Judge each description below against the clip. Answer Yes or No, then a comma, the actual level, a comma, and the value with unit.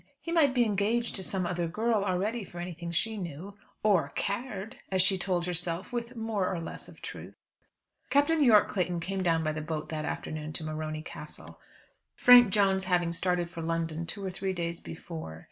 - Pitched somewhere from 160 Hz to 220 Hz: Yes, medium, 185 Hz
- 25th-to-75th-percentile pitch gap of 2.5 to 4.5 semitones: Yes, average, 3.9 semitones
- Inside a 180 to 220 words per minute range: Yes, average, 190 wpm